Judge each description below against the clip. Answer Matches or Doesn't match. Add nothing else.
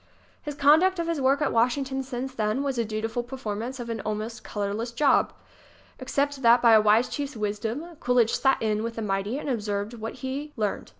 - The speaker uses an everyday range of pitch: Matches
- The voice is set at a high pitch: Matches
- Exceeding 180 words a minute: Matches